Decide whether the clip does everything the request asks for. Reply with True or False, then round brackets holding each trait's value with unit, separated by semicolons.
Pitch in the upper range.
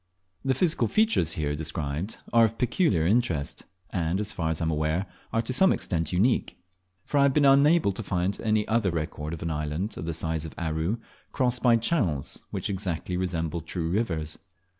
False (90 Hz)